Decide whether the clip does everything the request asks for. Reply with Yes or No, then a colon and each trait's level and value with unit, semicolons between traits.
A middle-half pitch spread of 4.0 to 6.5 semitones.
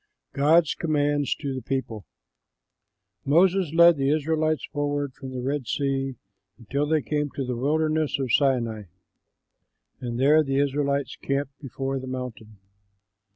No: narrow, 2.4 semitones